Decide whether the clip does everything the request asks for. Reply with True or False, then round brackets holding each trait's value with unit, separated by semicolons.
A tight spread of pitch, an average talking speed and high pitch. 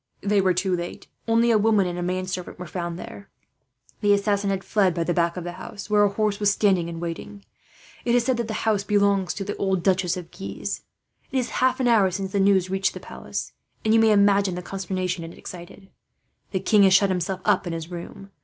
False (2.3 semitones; 230 wpm; 195 Hz)